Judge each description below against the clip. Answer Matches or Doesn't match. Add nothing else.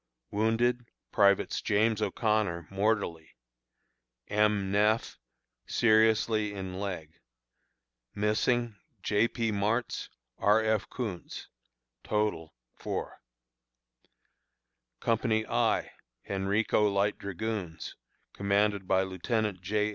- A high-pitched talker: Doesn't match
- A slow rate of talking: Matches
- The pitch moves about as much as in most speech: Doesn't match